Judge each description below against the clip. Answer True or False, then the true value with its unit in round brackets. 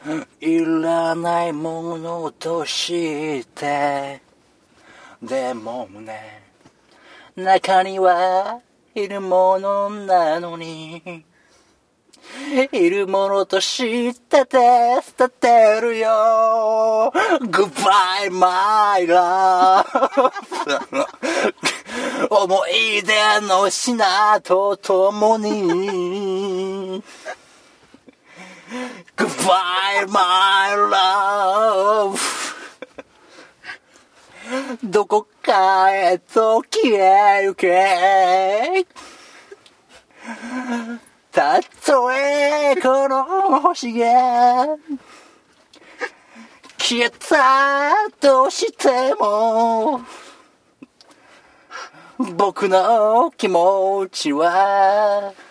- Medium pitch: False (210 Hz)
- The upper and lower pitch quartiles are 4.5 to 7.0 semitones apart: True (5.3 semitones)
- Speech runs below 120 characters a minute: True (105 characters per minute)